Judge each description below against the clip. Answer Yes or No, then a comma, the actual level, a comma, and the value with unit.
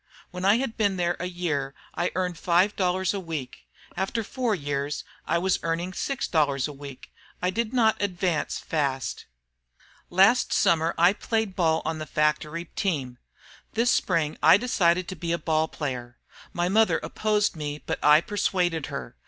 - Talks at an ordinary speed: Yes, average, 160 wpm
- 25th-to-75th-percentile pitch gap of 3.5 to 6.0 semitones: Yes, average, 4.2 semitones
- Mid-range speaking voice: Yes, medium, 175 Hz